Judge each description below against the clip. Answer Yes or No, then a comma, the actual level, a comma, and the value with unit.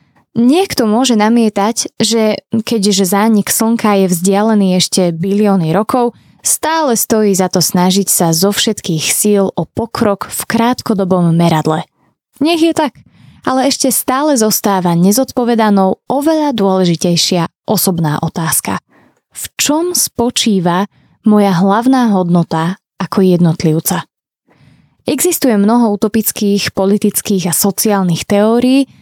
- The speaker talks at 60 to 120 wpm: Yes, slow, 110 wpm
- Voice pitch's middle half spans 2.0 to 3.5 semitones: No, average, 4.2 semitones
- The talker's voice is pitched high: Yes, high, 205 Hz